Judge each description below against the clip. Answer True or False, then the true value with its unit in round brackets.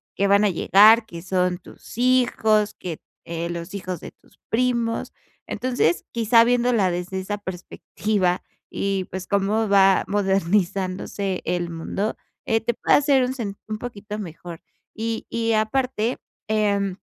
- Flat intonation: False (3.5 semitones)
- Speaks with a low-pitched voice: False (200 Hz)